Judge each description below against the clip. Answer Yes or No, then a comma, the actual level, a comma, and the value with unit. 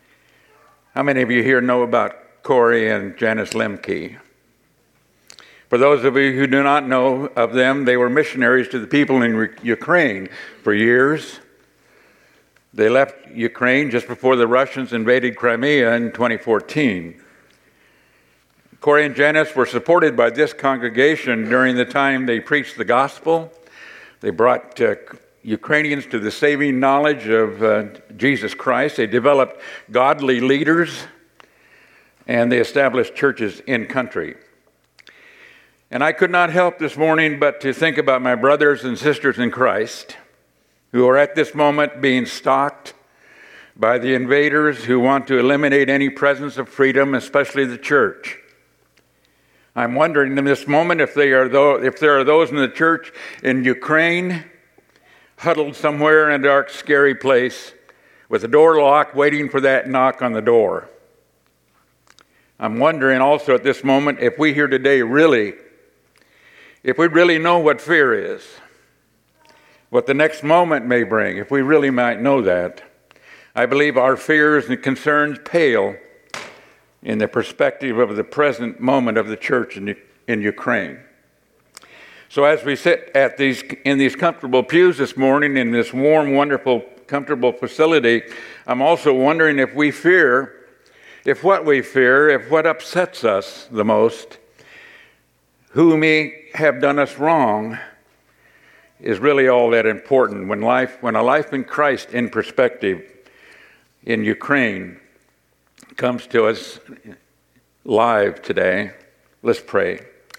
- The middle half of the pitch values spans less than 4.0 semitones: Yes, average, 3.5 semitones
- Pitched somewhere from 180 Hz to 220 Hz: No, medium, 140 Hz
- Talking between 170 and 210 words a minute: No, average, 145 wpm